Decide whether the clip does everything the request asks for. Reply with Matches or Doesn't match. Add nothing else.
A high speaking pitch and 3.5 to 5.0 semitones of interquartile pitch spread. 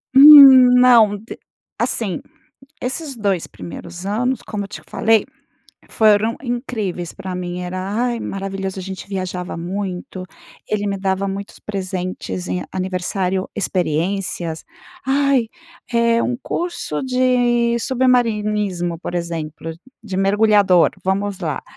Matches